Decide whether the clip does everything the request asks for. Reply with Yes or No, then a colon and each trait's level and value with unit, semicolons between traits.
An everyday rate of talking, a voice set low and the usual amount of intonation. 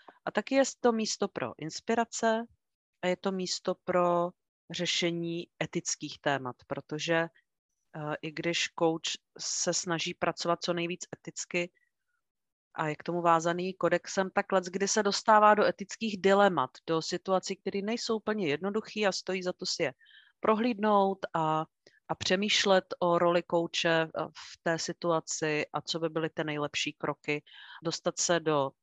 No: average, 150 wpm; medium, 175 Hz; average, 3.3 semitones